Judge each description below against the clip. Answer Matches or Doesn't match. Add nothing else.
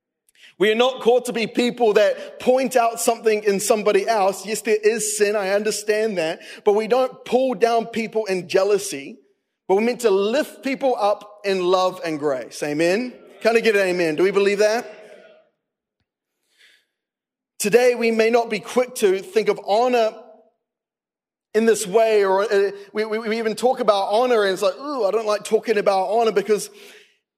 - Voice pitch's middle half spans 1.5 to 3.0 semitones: Matches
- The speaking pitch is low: Doesn't match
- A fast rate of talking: Doesn't match